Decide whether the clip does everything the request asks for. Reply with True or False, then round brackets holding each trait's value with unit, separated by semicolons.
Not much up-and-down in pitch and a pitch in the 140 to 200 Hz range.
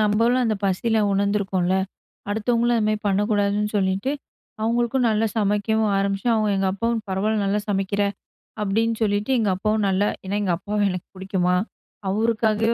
False (2.2 semitones; 210 Hz)